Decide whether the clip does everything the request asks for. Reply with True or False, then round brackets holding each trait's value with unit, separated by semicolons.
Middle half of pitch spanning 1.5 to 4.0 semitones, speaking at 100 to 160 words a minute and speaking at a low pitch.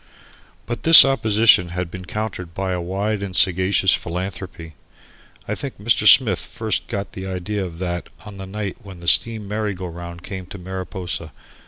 False (2.8 semitones; 175 wpm; 95 Hz)